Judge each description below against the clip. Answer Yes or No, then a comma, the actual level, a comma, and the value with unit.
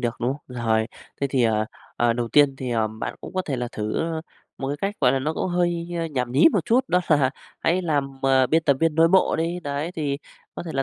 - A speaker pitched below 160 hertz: Yes, medium, 140 Hz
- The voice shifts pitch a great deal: No, average, 5.0 semitones